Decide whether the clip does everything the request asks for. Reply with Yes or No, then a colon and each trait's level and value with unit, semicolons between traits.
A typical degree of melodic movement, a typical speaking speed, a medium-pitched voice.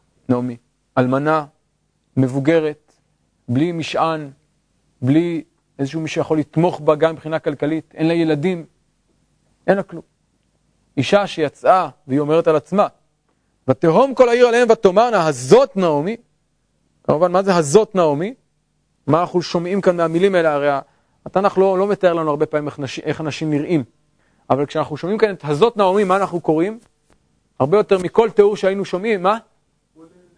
Yes: average, 4.0 semitones; average, 145 wpm; medium, 165 Hz